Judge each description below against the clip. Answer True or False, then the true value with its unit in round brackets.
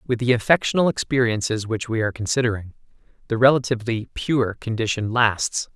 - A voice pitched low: True (115 Hz)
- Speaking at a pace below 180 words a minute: True (135 wpm)